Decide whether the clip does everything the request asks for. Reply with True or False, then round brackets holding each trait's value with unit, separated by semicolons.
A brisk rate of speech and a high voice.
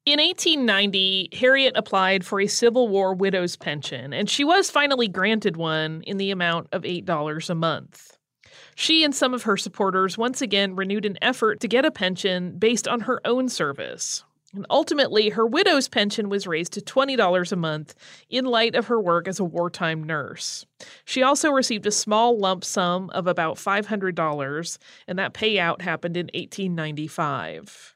False (170 wpm; 200 Hz)